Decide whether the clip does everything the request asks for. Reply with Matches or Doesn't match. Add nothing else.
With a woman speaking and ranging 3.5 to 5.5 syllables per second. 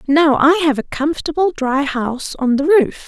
Matches